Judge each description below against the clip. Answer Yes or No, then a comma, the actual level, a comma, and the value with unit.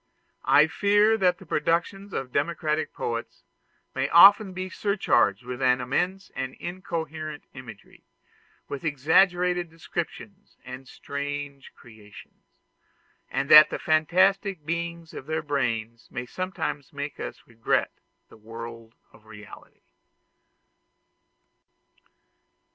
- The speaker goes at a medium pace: No, slow, 105 wpm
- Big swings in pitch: Yes, wide, 5.9 semitones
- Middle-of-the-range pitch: Yes, medium, 150 Hz